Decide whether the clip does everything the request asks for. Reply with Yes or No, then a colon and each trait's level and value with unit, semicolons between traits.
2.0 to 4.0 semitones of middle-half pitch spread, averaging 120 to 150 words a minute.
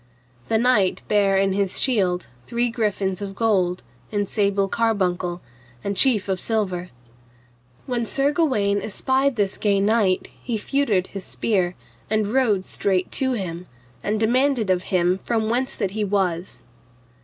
Yes: average, 3.4 semitones; average, 145 wpm